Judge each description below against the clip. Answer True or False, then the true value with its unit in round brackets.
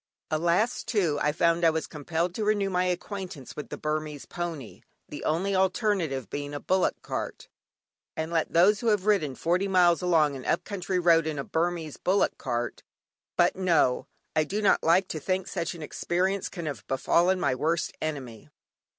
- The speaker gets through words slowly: False (180 wpm)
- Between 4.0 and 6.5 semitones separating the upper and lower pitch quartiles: False (3.6 semitones)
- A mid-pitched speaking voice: True (170 Hz)